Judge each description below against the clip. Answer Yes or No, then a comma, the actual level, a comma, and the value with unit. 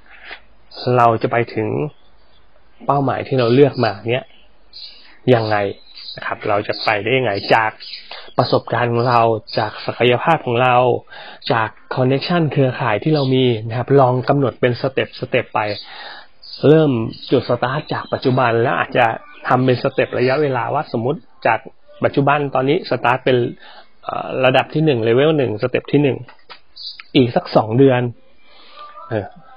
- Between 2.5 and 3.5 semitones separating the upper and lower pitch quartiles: Yes, average, 2.9 semitones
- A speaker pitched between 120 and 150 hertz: Yes, low, 125 Hz